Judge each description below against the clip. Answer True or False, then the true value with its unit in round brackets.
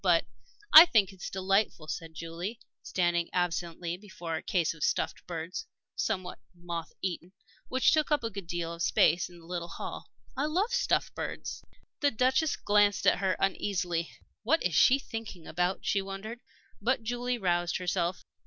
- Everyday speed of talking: True (170 wpm)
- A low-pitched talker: False (185 Hz)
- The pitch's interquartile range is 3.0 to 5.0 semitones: True (4.7 semitones)